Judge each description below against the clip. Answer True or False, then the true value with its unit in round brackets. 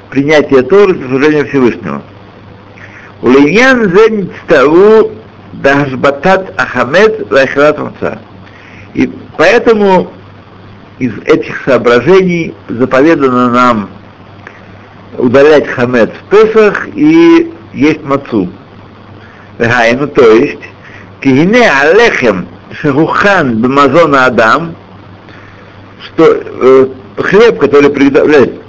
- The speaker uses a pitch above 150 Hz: False (135 Hz)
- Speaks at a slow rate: True (85 wpm)